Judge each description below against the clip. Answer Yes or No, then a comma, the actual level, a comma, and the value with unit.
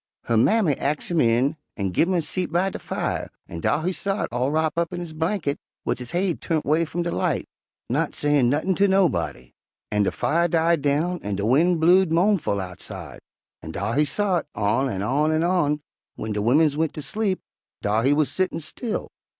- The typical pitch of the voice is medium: Yes, medium, 155 Hz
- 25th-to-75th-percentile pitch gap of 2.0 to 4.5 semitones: No, average, 5.3 semitones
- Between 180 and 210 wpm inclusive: Yes, fast, 205 wpm